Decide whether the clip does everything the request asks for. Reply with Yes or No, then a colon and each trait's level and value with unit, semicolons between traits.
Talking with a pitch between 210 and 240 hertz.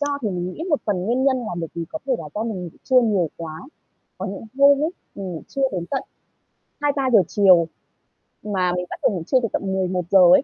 No: high, 195 Hz